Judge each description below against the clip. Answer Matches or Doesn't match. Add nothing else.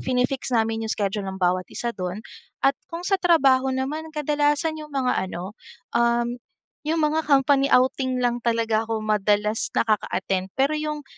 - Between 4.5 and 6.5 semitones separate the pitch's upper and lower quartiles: Matches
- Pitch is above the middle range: Matches